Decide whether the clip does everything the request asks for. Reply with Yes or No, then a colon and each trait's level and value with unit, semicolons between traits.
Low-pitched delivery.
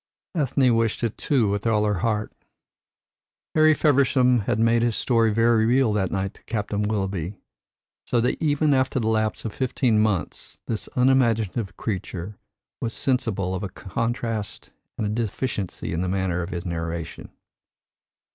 Yes: low, 110 Hz